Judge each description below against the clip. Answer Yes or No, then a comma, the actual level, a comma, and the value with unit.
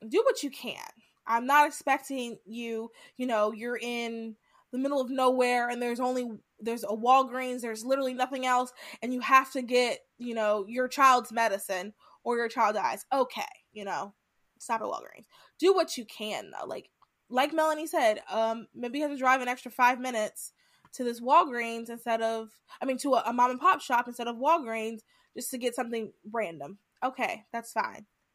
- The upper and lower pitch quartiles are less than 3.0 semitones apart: Yes, narrow, 2.6 semitones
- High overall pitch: Yes, high, 245 Hz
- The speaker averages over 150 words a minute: Yes, average, 190 wpm